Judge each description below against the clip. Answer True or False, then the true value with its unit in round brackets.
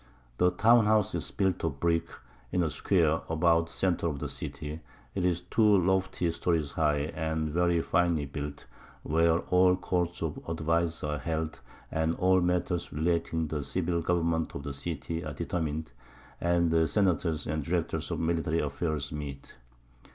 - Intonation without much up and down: True (2.3 semitones)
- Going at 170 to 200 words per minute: False (160 wpm)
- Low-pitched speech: True (80 Hz)